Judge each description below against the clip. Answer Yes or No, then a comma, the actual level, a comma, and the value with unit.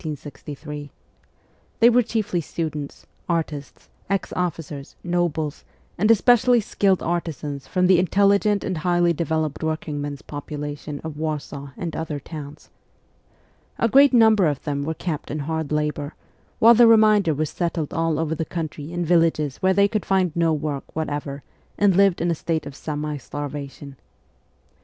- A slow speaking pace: No, average, 150 wpm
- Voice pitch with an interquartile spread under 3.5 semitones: No, average, 4.0 semitones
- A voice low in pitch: No, medium, 160 Hz